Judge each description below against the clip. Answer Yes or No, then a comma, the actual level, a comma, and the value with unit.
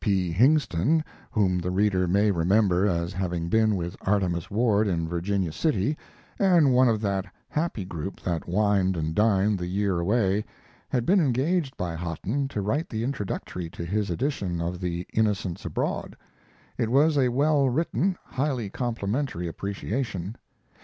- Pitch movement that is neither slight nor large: No, wide, 5.8 semitones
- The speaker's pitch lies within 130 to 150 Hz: No, low, 100 Hz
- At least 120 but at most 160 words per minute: Yes, average, 155 wpm